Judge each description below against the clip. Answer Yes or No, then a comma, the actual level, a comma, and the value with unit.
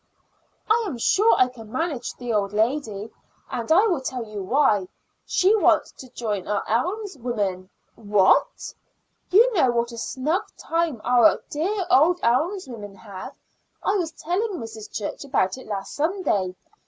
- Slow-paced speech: No, average, 155 wpm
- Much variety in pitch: Yes, wide, 8.3 semitones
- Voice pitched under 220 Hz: No, very high, 250 Hz